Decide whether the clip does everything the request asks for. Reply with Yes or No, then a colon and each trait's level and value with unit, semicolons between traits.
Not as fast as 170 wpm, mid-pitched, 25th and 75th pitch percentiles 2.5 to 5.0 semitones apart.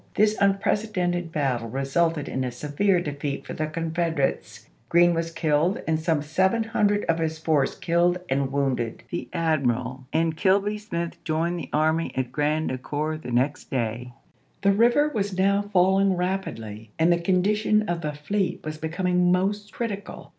Yes: average, 160 wpm; medium, 165 Hz; average, 4.5 semitones